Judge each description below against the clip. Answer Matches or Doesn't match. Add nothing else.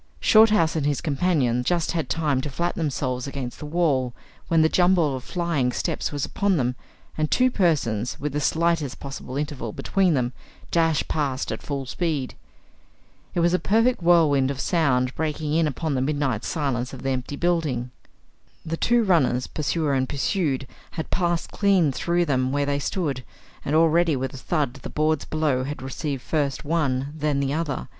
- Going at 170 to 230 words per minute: Matches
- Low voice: Doesn't match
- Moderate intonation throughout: Matches